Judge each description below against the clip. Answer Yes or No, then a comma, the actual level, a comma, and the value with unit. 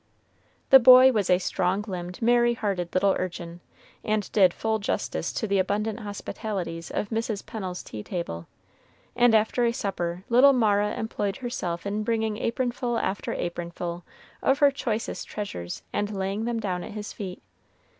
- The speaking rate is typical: Yes, average, 155 wpm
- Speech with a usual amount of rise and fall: Yes, average, 3.9 semitones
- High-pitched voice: Yes, high, 205 Hz